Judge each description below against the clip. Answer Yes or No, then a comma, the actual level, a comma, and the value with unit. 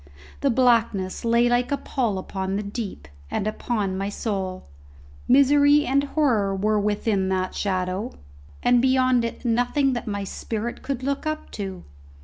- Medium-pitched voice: No, high, 230 Hz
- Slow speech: No, average, 150 wpm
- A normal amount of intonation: Yes, average, 4.7 semitones